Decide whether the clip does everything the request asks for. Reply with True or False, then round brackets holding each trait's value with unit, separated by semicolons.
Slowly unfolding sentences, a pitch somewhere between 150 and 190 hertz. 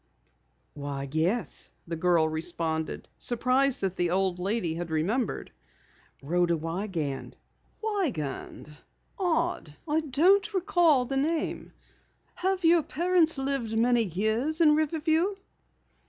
False (110 wpm; 235 Hz)